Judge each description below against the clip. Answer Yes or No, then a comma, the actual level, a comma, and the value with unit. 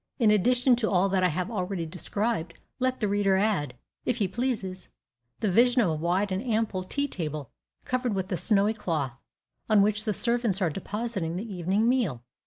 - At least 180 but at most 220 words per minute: Yes, average, 190 wpm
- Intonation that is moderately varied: Yes, average, 4.0 semitones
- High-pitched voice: Yes, high, 200 Hz